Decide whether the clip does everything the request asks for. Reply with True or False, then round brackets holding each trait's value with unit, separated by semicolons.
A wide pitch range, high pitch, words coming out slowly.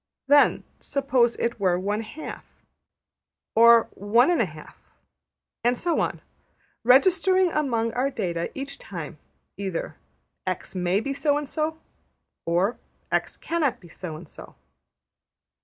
True (7.1 semitones; 235 Hz; 130 wpm)